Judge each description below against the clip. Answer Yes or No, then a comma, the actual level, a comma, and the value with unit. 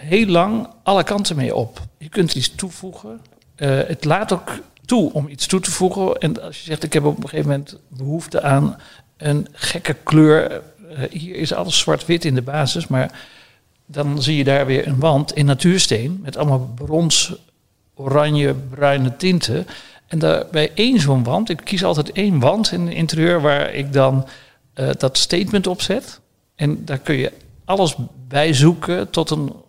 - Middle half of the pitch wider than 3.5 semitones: Yes, average, 4.1 semitones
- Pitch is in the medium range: Yes, medium, 150 Hz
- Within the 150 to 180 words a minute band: Yes, average, 175 wpm